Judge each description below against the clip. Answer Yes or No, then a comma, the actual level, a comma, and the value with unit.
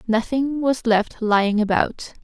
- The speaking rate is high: No, slow, 135 wpm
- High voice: Yes, high, 230 Hz